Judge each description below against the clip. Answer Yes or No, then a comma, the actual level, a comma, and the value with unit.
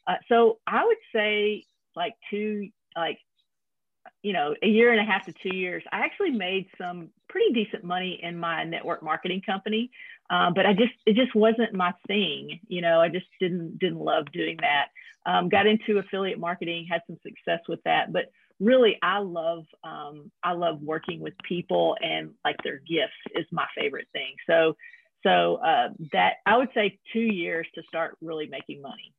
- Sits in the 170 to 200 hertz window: Yes, medium, 185 Hz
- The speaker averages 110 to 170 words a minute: No, average, 185 wpm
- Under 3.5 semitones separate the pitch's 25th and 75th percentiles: No, average, 4.5 semitones